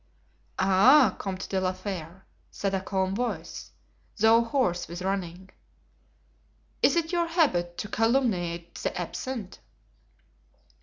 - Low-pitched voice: No, high, 195 Hz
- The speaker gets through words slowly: Yes, slow, 115 wpm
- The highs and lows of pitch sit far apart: No, average, 4.5 semitones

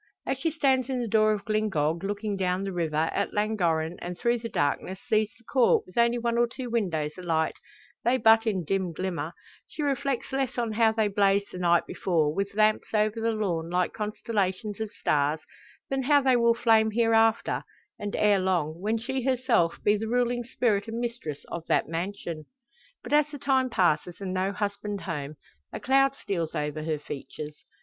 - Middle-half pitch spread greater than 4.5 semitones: Yes, average, 4.9 semitones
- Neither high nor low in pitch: No, high, 210 Hz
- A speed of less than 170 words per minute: No, average, 190 wpm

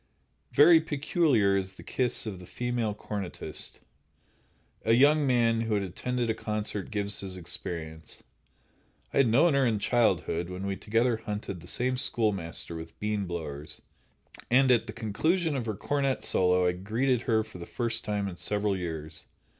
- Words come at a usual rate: Yes, average, 165 wpm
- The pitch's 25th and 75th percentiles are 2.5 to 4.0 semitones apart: No, average, 4.8 semitones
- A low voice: Yes, low, 105 Hz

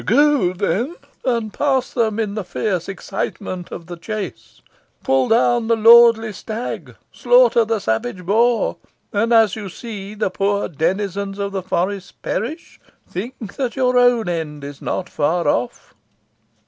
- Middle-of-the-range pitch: No, high, 205 Hz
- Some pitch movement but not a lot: Yes, average, 4.3 semitones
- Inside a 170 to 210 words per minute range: No, average, 150 wpm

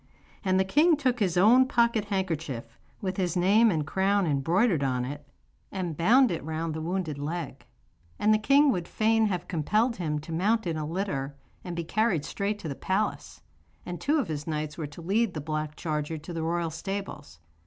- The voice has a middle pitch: Yes, medium, 175 Hz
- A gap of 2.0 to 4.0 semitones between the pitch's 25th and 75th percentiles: No, average, 5.3 semitones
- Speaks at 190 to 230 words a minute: Yes, average, 195 wpm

